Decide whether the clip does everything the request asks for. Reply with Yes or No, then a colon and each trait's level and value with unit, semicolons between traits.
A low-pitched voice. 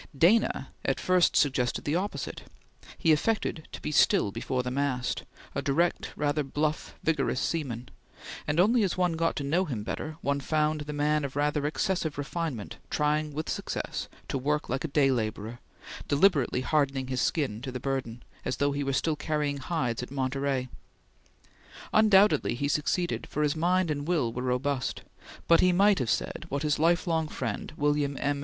No: medium, 145 Hz